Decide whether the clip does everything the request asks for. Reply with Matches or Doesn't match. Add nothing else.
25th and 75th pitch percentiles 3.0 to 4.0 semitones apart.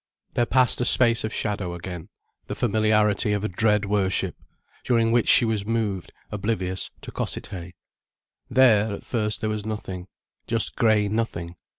Doesn't match